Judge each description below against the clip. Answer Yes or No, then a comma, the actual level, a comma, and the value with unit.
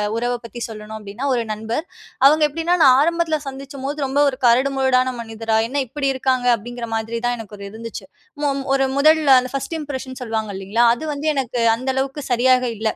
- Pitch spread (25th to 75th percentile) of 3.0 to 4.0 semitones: Yes, average, 3.4 semitones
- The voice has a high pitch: Yes, very high, 255 Hz